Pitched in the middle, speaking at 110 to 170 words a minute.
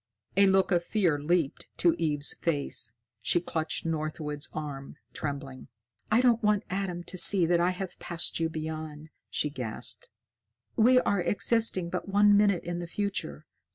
Yes: medium, 170 Hz; average, 155 wpm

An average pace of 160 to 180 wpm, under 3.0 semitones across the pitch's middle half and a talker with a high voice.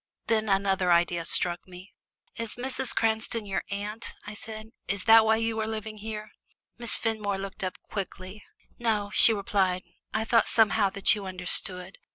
Yes: average, 165 wpm; narrow, 2.5 semitones; high, 210 Hz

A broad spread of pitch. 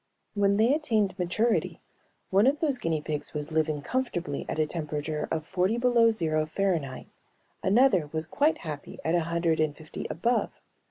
Yes: wide, 6.4 semitones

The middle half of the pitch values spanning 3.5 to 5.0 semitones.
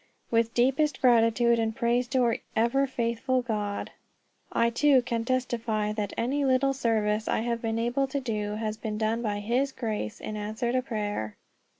No: average, 2.8 semitones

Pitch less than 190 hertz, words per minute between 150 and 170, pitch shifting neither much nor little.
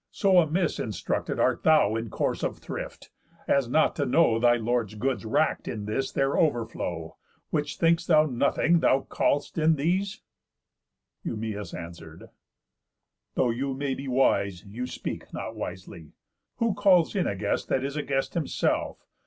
No: low, 135 Hz; average, 160 wpm; wide, 6.4 semitones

